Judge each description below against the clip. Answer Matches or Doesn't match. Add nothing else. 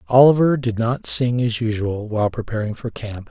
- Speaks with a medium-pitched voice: Doesn't match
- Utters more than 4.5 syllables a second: Matches